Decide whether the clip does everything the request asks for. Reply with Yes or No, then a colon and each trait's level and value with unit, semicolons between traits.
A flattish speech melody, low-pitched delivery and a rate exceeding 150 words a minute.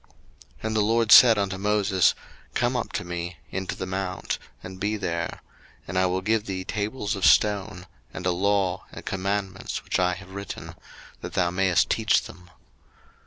Yes: narrow, 2.1 semitones; very low, 95 Hz; average, 175 wpm